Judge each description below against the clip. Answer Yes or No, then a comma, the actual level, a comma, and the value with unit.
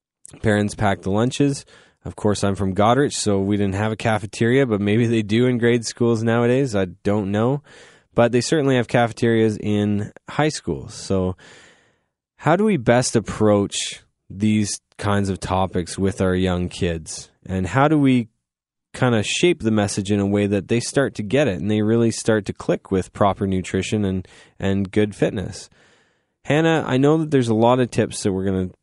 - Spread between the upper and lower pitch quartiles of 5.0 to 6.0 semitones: No, average, 3.6 semitones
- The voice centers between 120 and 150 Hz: No, low, 105 Hz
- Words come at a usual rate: Yes, average, 190 wpm